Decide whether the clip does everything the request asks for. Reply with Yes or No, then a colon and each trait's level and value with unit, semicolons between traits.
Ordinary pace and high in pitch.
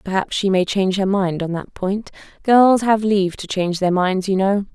No: fast, 230 wpm; high, 195 Hz